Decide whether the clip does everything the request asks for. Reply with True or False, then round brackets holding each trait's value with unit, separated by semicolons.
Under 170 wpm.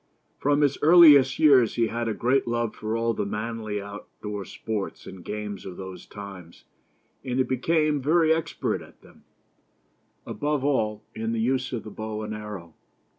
False (175 wpm)